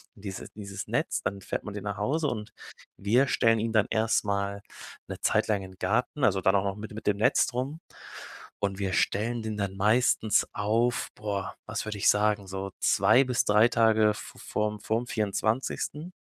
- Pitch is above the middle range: No, low, 105 Hz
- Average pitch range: No, narrow, 2.2 semitones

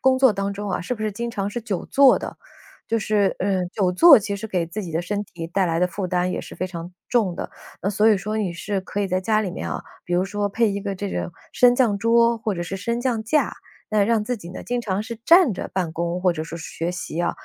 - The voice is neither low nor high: No, high, 200 Hz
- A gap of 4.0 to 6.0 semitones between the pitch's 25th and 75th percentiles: No, average, 3.5 semitones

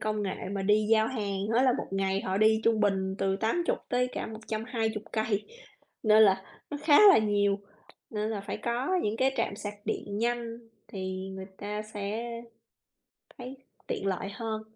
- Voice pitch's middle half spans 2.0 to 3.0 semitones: Yes, narrow, 2.4 semitones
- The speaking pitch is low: No, high, 215 Hz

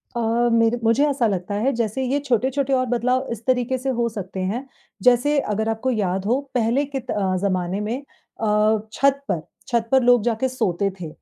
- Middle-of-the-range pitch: No, high, 235 Hz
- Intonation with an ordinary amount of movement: Yes, average, 3.6 semitones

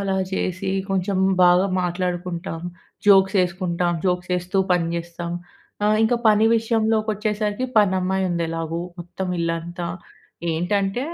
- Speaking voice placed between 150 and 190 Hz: Yes, medium, 185 Hz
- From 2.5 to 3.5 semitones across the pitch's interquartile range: Yes, average, 2.9 semitones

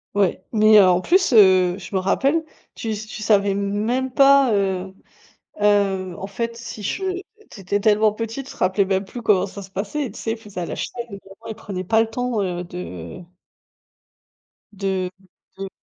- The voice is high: Yes, high, 205 Hz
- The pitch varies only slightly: No, average, 3.1 semitones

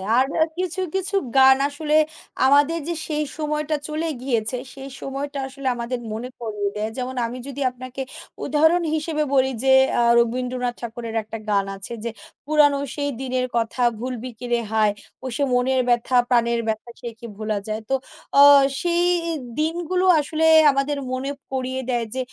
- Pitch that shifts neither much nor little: Yes, average, 3.8 semitones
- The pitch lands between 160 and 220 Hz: No, very high, 260 Hz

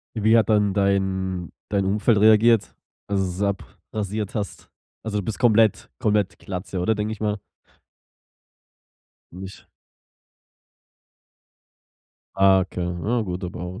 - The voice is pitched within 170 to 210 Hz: No, low, 100 Hz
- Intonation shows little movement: Yes, narrow, 2.3 semitones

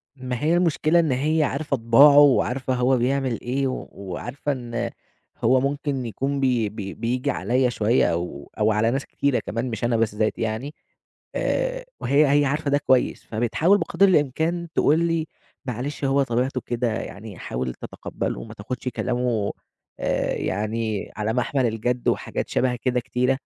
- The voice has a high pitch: No, low, 125 Hz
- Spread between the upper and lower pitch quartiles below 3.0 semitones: No, average, 3.7 semitones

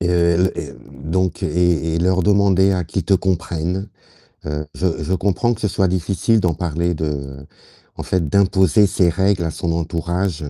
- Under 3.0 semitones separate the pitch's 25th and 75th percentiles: Yes, narrow, 2.4 semitones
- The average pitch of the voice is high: No, very low, 90 Hz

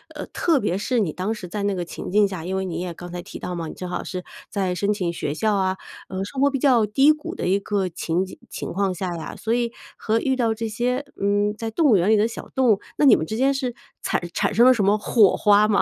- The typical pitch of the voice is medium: No, high, 205 Hz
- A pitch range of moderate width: Yes, average, 4.0 semitones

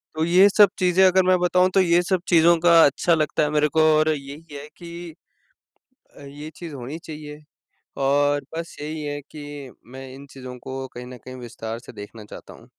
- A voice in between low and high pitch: Yes, medium, 150 Hz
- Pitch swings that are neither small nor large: Yes, average, 3.7 semitones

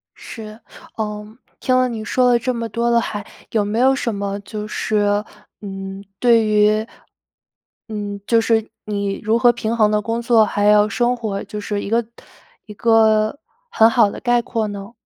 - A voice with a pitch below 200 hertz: No, high, 215 Hz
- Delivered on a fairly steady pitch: Yes, narrow, 2.0 semitones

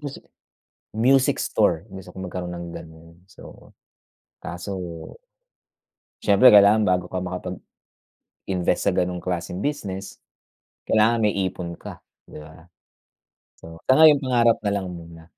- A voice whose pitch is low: Yes, very low, 95 Hz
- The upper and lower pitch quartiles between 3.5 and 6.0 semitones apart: Yes, average, 4.0 semitones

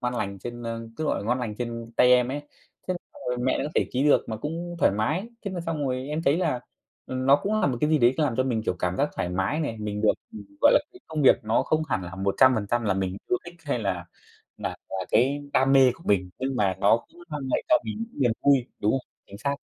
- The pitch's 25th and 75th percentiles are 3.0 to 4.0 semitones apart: No, wide, 5.4 semitones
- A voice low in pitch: Yes, low, 125 Hz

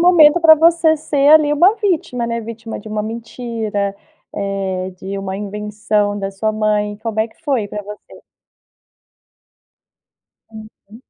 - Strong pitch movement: Yes, wide, 5.7 semitones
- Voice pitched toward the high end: Yes, high, 220 Hz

